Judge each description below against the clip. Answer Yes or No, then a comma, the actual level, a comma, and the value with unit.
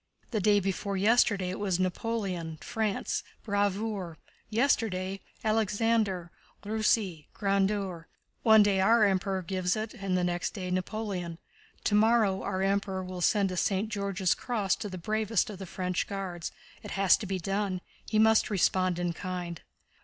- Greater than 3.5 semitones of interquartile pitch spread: No, average, 2.7 semitones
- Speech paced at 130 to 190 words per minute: Yes, average, 145 wpm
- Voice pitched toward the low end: No, high, 195 Hz